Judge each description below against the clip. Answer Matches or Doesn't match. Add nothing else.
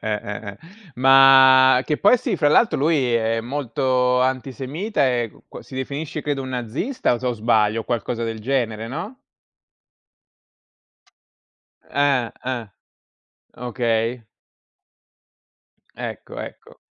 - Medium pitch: Doesn't match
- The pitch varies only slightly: Doesn't match